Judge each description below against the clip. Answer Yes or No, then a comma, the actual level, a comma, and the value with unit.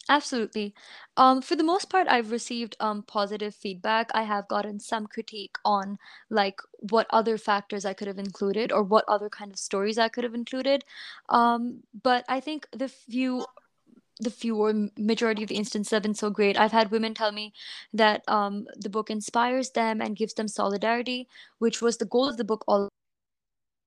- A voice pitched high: Yes, high, 220 Hz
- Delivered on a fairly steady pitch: Yes, narrow, 2.3 semitones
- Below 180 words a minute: No, average, 185 wpm